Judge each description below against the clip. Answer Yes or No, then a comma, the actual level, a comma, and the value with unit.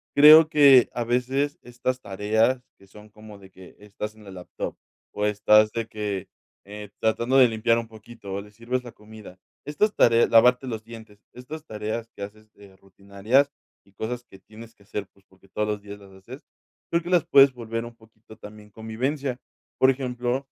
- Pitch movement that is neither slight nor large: Yes, average, 3.2 semitones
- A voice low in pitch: Yes, low, 110 Hz